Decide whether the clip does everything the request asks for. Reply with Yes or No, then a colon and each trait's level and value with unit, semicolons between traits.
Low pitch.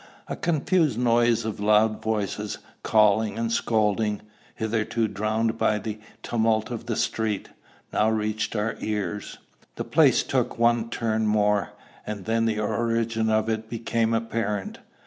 Yes: low, 110 Hz